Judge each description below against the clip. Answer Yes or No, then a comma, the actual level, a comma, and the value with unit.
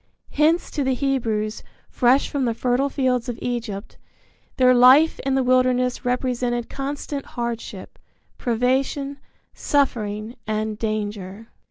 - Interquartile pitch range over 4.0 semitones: No, average, 3.0 semitones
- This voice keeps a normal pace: No, slow, 120 wpm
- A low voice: No, very high, 250 Hz